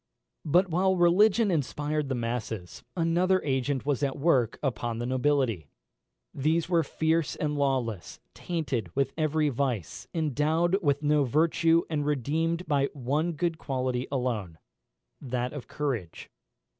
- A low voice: No, medium, 145 Hz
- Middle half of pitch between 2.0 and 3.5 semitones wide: No, average, 4.3 semitones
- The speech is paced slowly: Yes, slow, 130 wpm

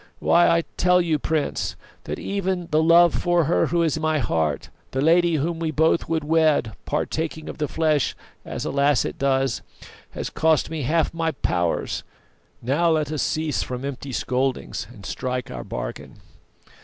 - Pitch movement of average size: Yes, average, 3.6 semitones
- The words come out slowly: No, average, 170 wpm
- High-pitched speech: No, medium, 155 Hz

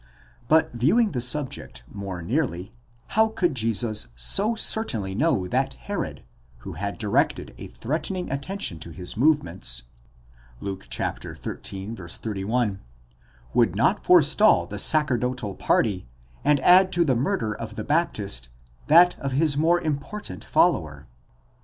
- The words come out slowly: Yes, slow, 130 wpm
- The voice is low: Yes, low, 125 Hz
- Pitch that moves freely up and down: Yes, wide, 8.3 semitones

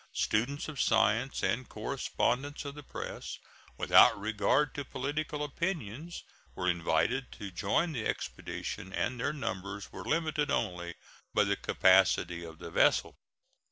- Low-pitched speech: Yes, low, 120 Hz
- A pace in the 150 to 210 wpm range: No, slow, 135 wpm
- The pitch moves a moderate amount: No, wide, 7.0 semitones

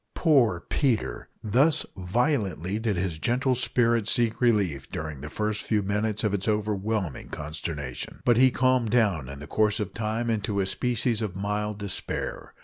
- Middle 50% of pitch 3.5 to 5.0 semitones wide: Yes, average, 3.8 semitones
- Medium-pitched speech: No, low, 105 Hz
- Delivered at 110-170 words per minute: Yes, average, 160 wpm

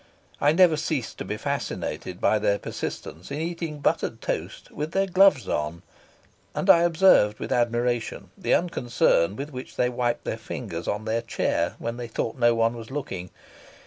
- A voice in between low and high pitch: No, low, 120 Hz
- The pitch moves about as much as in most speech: No, wide, 6.1 semitones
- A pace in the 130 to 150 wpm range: No, average, 175 wpm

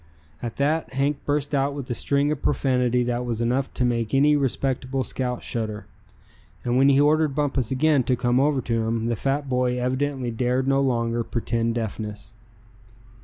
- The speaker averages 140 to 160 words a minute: No, average, 175 wpm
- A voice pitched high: No, low, 130 Hz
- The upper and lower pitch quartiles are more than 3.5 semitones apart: No, average, 2.8 semitones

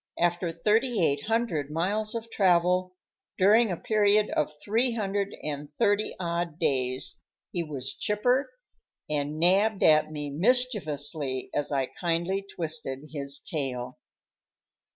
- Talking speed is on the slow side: Yes, slow, 125 wpm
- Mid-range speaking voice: Yes, medium, 175 Hz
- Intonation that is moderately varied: No, wide, 5.9 semitones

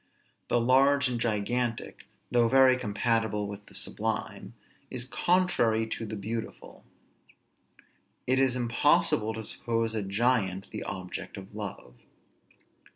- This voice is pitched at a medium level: No, low, 115 Hz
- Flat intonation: No, average, 3.1 semitones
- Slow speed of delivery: Yes, slow, 120 wpm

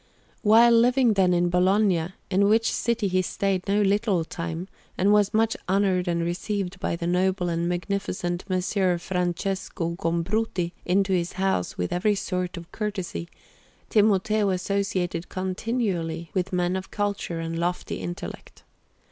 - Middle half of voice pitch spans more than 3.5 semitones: No, narrow, 2.6 semitones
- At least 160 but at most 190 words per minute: No, average, 140 wpm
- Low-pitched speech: No, medium, 185 Hz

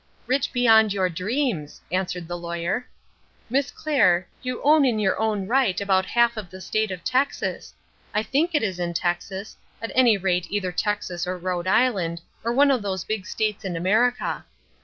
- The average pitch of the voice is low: No, high, 205 Hz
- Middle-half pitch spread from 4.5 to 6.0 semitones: Yes, average, 5.0 semitones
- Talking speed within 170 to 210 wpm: Yes, average, 180 wpm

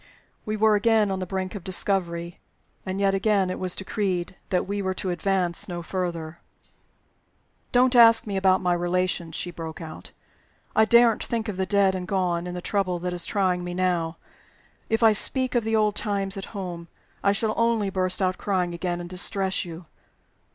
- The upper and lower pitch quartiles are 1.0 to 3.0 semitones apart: Yes, narrow, 2.6 semitones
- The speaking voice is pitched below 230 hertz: Yes, high, 190 Hz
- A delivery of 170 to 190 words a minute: Yes, average, 185 wpm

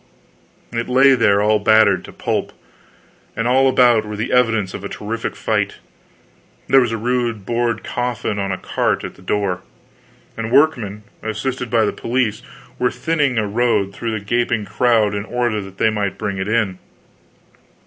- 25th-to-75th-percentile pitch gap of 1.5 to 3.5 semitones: Yes, average, 2.9 semitones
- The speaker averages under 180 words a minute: Yes, average, 170 wpm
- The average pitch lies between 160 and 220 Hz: No, low, 110 Hz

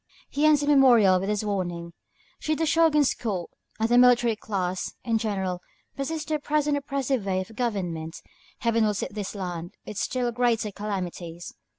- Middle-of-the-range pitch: No, high, 220 Hz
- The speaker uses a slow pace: No, average, 175 wpm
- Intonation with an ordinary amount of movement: No, wide, 6.3 semitones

